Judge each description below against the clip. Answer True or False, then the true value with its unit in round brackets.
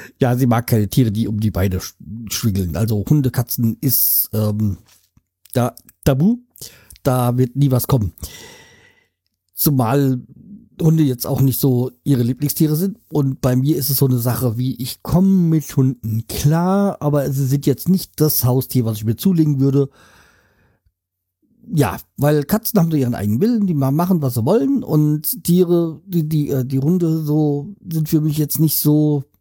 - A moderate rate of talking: True (170 wpm)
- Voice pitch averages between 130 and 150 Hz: True (135 Hz)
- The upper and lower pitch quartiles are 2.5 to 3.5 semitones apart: False (5.4 semitones)